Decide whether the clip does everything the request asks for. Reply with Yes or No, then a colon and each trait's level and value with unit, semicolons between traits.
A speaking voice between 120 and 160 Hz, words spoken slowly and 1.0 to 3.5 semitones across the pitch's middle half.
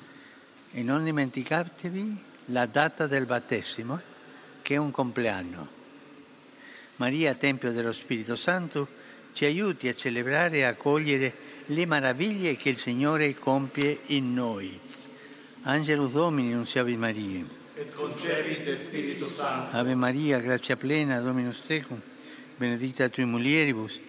Yes: low, 135 Hz; slow, 115 wpm; average, 3.1 semitones